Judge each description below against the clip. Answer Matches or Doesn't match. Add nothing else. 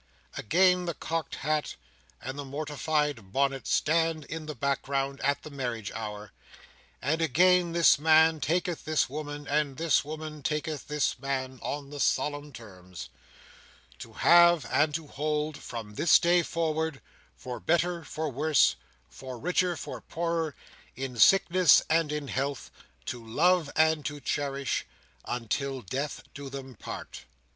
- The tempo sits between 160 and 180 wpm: Doesn't match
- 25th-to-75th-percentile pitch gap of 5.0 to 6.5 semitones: Doesn't match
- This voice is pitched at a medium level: Matches